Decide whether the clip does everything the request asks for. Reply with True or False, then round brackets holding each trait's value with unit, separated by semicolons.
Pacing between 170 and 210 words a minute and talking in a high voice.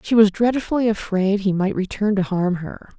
True (200 wpm; 200 Hz)